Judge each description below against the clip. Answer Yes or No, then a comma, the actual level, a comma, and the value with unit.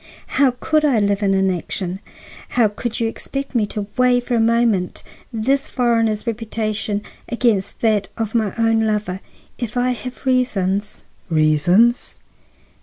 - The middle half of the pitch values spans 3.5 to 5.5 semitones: No, average, 3.0 semitones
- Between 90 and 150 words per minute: Yes, average, 140 wpm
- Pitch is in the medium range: No, high, 225 Hz